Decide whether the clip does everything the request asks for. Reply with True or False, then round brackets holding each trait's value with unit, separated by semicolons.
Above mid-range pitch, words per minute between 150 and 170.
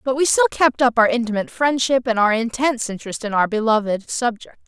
False (240 Hz; 205 wpm)